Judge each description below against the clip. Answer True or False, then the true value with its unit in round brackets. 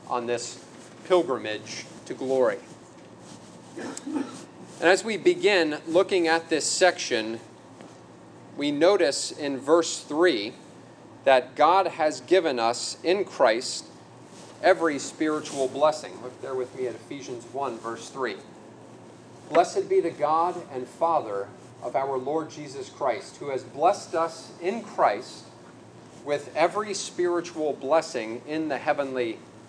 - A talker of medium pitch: True (155 Hz)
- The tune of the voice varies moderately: False (5.7 semitones)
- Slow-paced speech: True (125 wpm)